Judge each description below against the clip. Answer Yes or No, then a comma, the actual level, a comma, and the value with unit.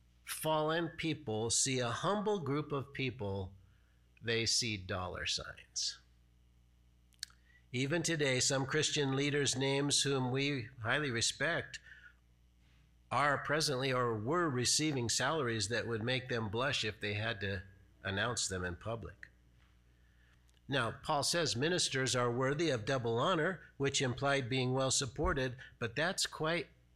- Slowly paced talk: Yes, slow, 130 wpm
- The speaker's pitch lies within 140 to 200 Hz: No, low, 120 Hz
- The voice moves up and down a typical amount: No, wide, 6.2 semitones